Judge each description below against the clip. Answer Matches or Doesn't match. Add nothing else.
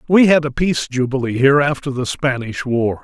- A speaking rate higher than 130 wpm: Matches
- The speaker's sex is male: Matches